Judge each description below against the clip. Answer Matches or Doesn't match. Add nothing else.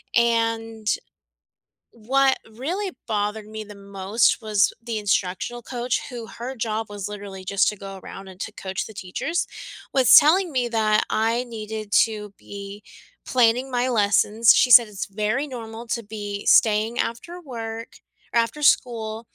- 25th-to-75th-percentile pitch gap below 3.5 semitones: Matches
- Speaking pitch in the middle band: Doesn't match